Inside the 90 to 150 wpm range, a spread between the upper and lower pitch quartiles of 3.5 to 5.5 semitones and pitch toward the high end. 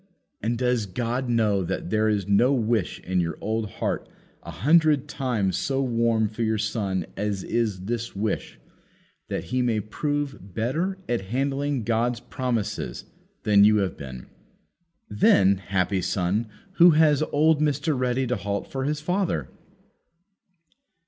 No: average, 145 wpm; average, 4.9 semitones; low, 115 Hz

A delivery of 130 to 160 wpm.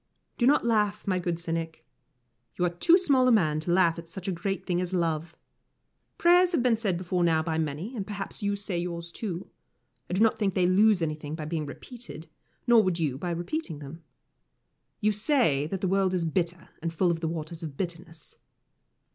No: average, 200 wpm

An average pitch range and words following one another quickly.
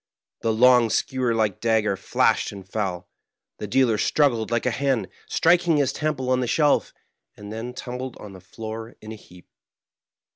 No: average, 3.5 semitones; average, 175 wpm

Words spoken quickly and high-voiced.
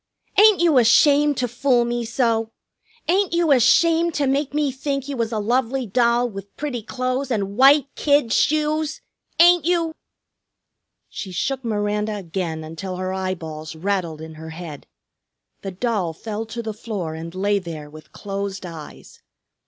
No: average, 155 wpm; high, 230 Hz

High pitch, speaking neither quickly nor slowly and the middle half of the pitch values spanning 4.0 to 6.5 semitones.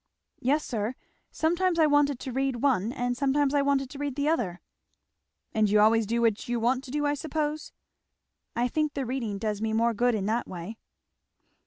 Yes: very high, 255 Hz; average, 195 wpm; average, 4.4 semitones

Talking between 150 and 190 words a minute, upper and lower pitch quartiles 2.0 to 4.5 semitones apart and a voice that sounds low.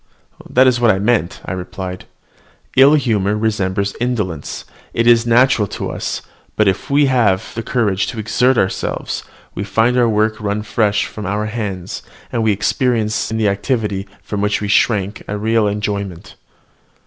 Yes: average, 165 wpm; average, 2.8 semitones; low, 105 Hz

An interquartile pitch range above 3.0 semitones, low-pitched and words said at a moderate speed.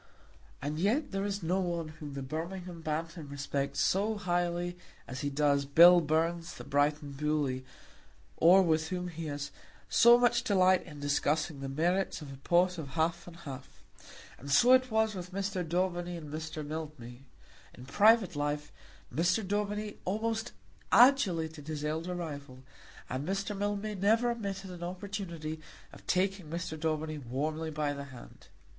No: average, 4.5 semitones; medium, 170 Hz; average, 155 wpm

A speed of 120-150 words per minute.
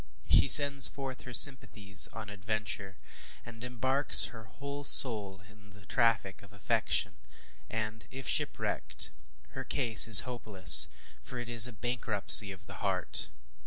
Yes: average, 140 wpm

